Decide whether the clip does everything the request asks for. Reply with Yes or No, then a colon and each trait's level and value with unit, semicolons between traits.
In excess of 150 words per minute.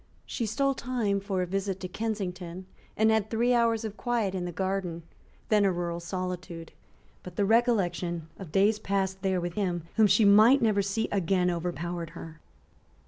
Yes: average, 175 wpm